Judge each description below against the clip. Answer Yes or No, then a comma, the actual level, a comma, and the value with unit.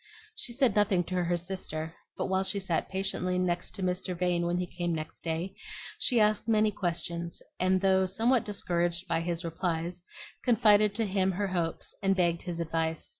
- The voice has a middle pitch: Yes, medium, 180 Hz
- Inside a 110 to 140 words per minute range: No, average, 175 wpm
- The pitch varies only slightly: Yes, narrow, 2.3 semitones